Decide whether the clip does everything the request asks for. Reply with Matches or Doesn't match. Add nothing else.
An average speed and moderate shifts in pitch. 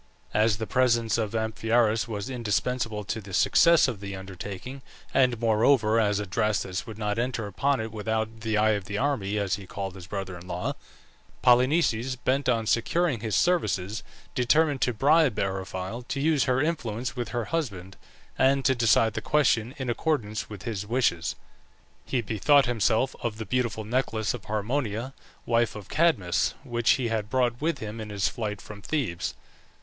Matches